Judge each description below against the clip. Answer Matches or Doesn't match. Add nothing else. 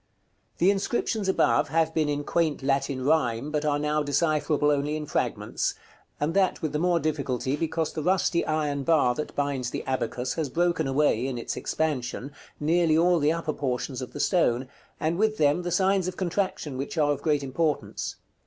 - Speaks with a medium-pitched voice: Matches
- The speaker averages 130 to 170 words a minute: Doesn't match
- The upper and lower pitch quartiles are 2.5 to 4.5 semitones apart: Matches